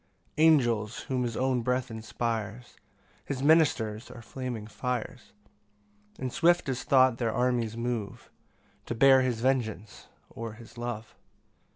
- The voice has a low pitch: Yes, low, 120 Hz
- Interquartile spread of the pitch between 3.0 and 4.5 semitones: No, narrow, 2.5 semitones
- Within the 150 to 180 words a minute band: No, slow, 135 wpm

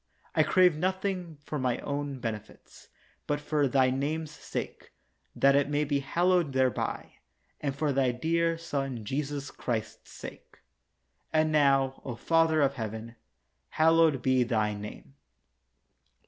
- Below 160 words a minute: Yes, slow, 135 wpm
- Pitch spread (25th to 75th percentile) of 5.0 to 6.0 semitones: No, average, 3.5 semitones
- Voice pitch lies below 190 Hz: Yes, medium, 140 Hz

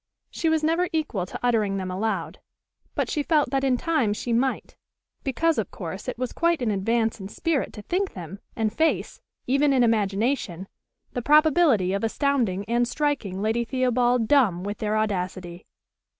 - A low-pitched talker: No, high, 235 Hz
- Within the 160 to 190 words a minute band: Yes, average, 170 wpm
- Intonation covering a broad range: Yes, wide, 5.8 semitones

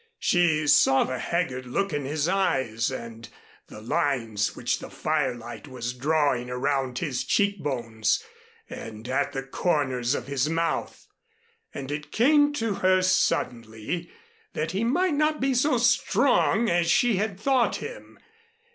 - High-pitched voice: No, medium, 145 Hz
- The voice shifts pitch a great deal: Yes, wide, 7.9 semitones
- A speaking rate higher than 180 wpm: No, average, 145 wpm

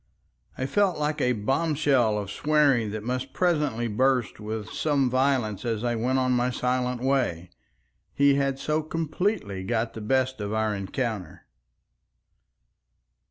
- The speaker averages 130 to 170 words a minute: Yes, average, 140 wpm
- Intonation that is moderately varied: Yes, average, 4.3 semitones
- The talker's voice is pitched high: No, low, 125 Hz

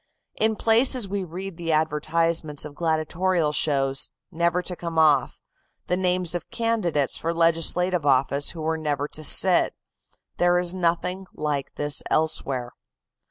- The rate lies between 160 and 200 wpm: No, average, 140 wpm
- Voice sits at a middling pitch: Yes, medium, 165 Hz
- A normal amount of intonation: Yes, average, 3.1 semitones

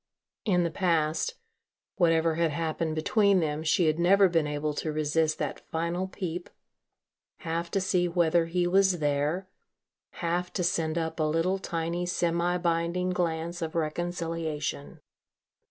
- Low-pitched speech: No, medium, 170 Hz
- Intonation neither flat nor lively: No, narrow, 1.9 semitones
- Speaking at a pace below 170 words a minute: Yes, average, 140 wpm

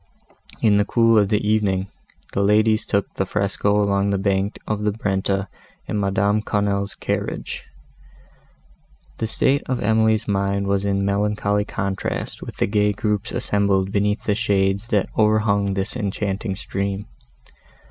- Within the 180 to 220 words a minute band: No, average, 145 wpm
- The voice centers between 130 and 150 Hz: No, low, 100 Hz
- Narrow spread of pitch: Yes, narrow, 1.3 semitones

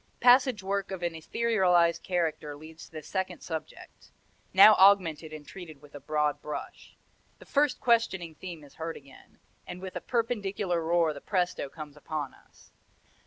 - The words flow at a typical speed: Yes, average, 165 wpm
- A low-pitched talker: No, medium, 175 Hz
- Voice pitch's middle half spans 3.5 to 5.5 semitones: Yes, average, 3.9 semitones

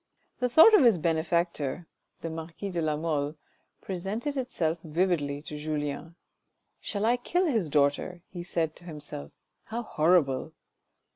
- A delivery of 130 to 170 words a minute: Yes, average, 165 wpm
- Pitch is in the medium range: Yes, medium, 170 Hz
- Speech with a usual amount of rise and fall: Yes, average, 4.8 semitones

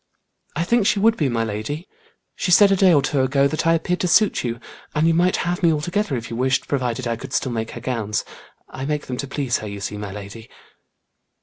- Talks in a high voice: No, medium, 140 Hz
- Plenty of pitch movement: Yes, wide, 6.5 semitones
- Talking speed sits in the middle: No, fast, 240 wpm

